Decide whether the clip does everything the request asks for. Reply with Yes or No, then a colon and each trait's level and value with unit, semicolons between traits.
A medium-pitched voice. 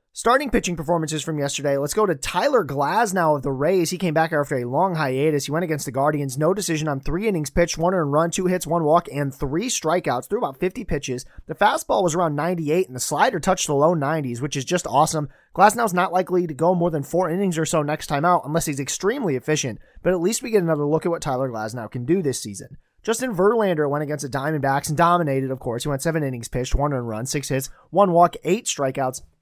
Yes: medium, 155 Hz